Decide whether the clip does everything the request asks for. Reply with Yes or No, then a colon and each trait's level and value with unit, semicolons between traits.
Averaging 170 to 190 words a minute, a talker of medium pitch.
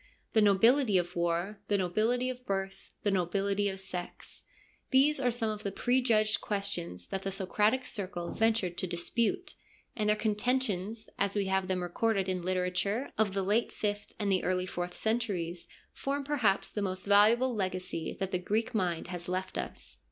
No: average, 180 wpm; high, 200 Hz